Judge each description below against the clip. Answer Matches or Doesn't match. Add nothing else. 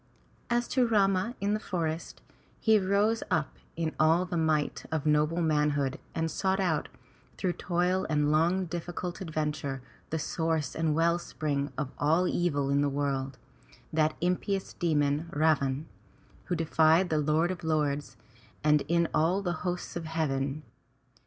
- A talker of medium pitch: Matches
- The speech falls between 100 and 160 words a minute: Matches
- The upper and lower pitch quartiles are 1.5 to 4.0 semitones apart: Matches